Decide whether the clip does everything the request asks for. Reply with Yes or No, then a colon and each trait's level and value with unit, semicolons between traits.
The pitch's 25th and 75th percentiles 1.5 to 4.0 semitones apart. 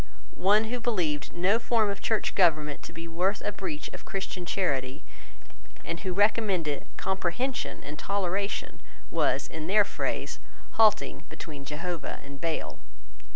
No: average, 4.7 semitones